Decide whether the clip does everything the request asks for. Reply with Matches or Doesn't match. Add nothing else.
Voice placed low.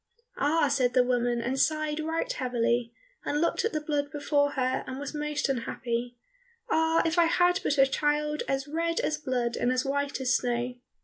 Doesn't match